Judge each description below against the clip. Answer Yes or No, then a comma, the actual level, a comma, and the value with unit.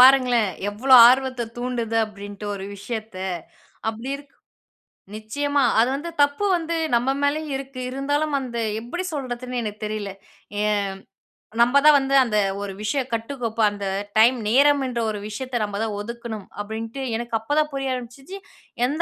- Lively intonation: No, average, 3.9 semitones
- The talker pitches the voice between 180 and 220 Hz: No, high, 245 Hz